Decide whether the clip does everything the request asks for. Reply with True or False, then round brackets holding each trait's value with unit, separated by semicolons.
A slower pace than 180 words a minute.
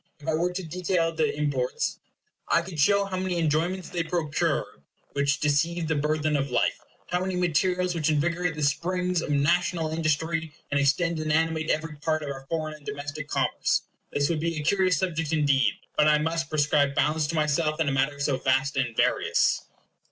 False (190 wpm)